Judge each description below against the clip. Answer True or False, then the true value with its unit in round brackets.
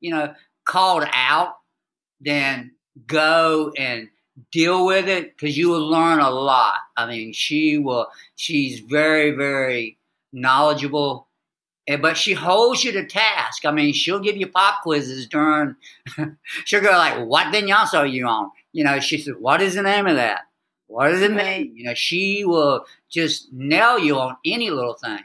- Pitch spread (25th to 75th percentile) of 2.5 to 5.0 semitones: True (4.7 semitones)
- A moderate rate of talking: True (170 wpm)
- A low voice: False (150 Hz)